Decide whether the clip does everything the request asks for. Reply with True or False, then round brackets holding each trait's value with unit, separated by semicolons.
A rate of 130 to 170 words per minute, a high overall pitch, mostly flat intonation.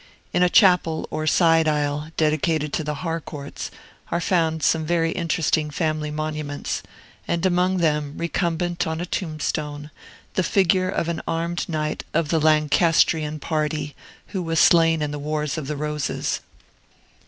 False (150 wpm; 160 Hz; 1.9 semitones)